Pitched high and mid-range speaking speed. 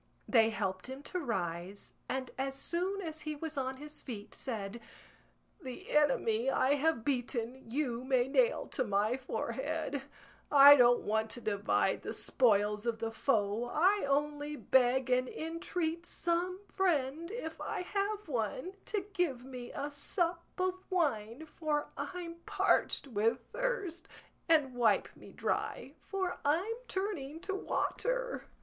Yes: very high, 280 Hz; average, 145 wpm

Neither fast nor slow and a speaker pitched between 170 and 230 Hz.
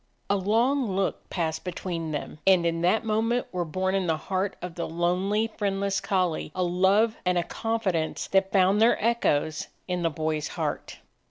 Yes: average, 175 wpm; medium, 185 Hz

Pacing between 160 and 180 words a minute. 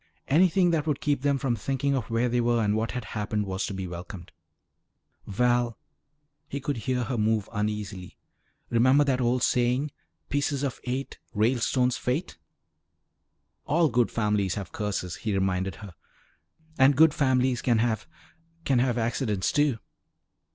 No: average, 150 wpm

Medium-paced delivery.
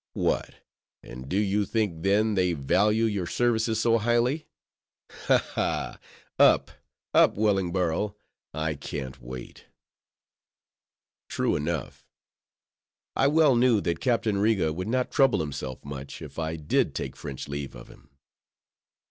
No: slow, 130 wpm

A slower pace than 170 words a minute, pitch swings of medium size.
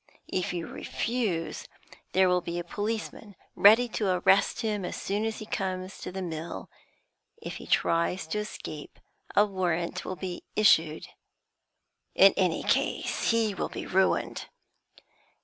Yes: average, 145 wpm; average, 3.3 semitones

